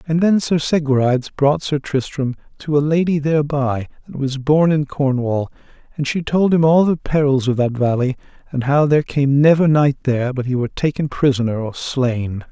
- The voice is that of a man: Yes, male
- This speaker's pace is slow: No, average, 190 wpm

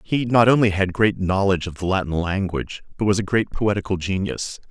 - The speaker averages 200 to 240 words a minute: Yes, fast, 205 wpm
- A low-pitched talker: Yes, very low, 95 Hz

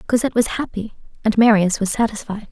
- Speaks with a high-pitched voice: Yes, high, 215 Hz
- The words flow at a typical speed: Yes, average, 165 wpm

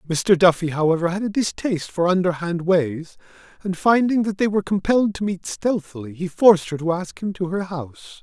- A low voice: No, medium, 180 Hz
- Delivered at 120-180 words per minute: No, average, 195 wpm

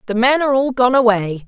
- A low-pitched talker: No, high, 245 Hz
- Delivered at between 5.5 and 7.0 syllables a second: Yes, 6.1 syllables/s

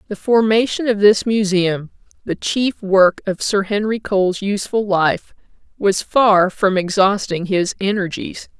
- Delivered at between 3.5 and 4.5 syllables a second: Yes, 4.2 syllables/s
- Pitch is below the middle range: No, high, 200 Hz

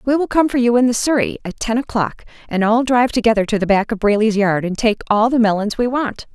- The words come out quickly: Yes, fast, 265 wpm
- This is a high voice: Yes, high, 225 Hz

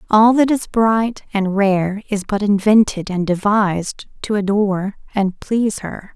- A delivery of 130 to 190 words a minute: Yes, average, 155 wpm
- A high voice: Yes, high, 205 Hz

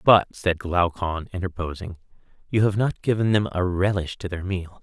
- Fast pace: No, average, 175 wpm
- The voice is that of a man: Yes, male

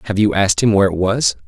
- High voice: No, very low, 95 Hz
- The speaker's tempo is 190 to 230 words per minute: No, fast, 285 wpm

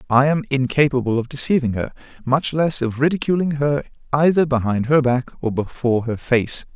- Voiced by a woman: No, male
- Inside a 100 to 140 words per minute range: No, average, 170 wpm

